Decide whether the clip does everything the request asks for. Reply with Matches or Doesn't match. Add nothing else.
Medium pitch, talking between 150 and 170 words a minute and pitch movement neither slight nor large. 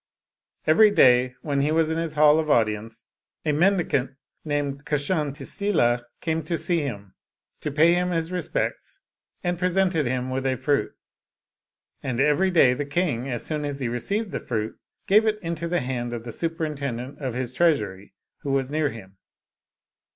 Matches